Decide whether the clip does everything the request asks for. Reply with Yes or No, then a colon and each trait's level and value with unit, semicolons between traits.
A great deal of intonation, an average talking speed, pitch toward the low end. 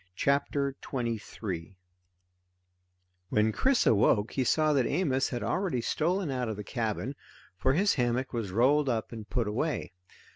No: average, 4.4 semitones; average, 145 wpm; low, 125 Hz